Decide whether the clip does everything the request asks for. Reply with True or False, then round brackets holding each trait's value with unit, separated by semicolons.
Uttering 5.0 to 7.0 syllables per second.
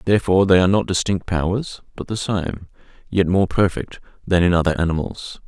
True (5.8 syllables/s)